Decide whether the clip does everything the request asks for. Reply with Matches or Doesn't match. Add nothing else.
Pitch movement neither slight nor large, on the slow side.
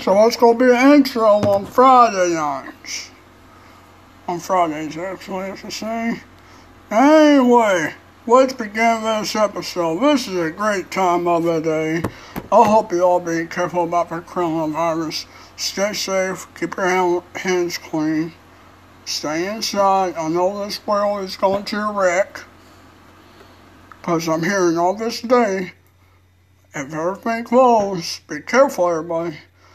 Matches